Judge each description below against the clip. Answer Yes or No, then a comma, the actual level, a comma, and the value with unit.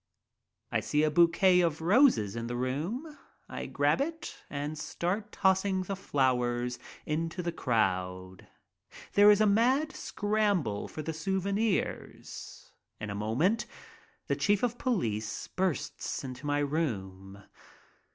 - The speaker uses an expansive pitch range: Yes, wide, 8.7 semitones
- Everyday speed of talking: No, slow, 130 wpm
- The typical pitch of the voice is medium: Yes, medium, 165 Hz